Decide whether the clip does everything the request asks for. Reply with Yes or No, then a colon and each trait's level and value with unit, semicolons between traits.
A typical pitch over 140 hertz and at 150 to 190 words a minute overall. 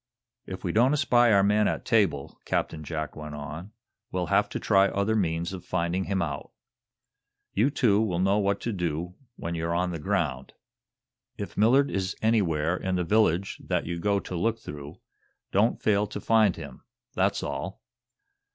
No: very low, 95 Hz; average, 175 wpm